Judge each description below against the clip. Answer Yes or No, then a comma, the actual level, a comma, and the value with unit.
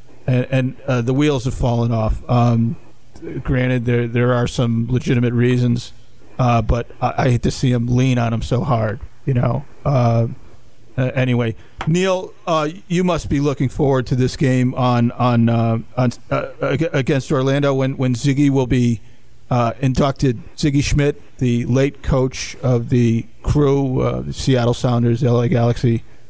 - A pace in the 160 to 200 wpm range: Yes, average, 165 wpm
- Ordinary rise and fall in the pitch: No, narrow, 2.1 semitones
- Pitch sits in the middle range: No, low, 125 Hz